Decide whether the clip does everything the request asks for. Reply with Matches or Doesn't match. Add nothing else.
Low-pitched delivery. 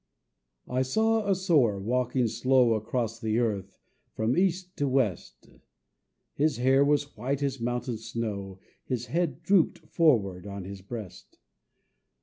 Matches